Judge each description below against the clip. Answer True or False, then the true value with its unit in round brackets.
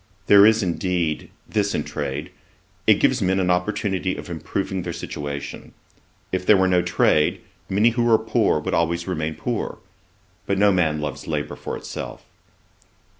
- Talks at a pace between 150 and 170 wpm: True (160 wpm)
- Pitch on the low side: True (90 Hz)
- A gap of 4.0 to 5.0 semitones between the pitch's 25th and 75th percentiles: True (4.3 semitones)